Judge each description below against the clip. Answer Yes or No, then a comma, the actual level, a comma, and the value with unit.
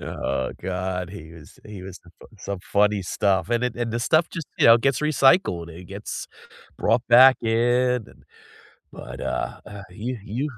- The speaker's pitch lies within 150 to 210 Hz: No, low, 105 Hz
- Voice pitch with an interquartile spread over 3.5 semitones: Yes, average, 5.2 semitones